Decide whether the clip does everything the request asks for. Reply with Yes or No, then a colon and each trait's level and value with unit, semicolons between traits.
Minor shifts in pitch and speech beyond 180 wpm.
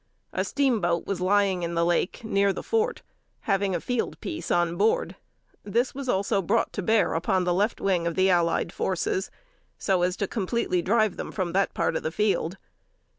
No: average, 3.6 semitones; average, 190 wpm